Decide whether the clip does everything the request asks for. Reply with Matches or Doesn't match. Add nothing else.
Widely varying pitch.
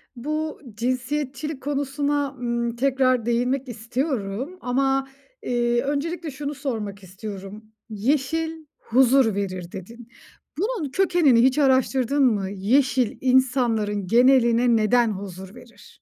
Doesn't match